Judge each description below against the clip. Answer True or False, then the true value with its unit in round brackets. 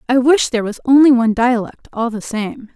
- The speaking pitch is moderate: False (240 Hz)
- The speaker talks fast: True (220 wpm)